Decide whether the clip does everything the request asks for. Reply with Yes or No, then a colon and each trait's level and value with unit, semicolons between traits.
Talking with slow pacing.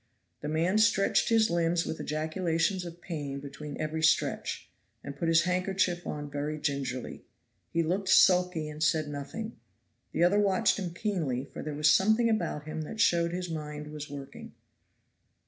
No: average, 165 wpm